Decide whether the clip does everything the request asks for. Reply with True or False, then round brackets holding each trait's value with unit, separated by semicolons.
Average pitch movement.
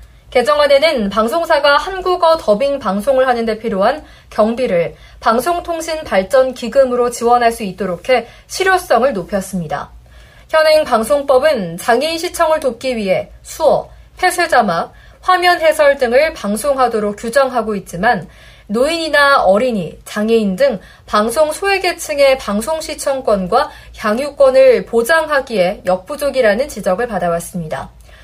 False (6.3 semitones)